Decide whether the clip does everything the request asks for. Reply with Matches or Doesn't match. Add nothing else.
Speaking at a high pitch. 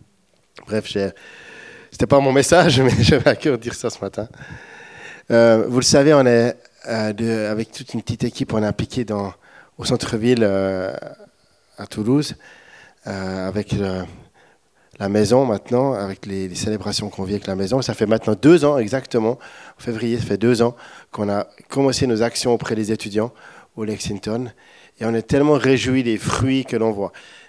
Doesn't match